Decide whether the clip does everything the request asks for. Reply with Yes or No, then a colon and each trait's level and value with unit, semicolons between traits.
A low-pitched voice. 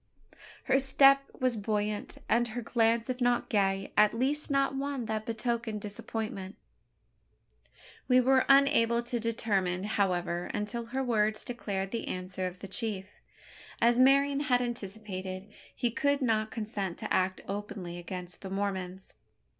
No: high, 220 Hz